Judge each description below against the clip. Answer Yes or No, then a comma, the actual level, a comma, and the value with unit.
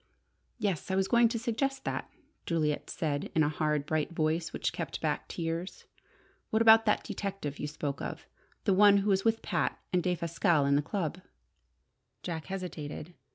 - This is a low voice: No, medium, 175 Hz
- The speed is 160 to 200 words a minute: Yes, average, 170 wpm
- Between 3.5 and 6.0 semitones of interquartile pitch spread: Yes, average, 4.7 semitones